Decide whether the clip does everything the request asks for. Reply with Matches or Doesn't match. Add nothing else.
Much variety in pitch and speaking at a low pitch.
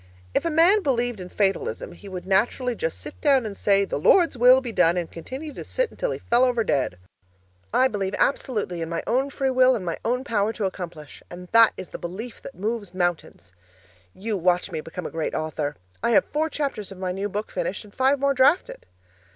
Doesn't match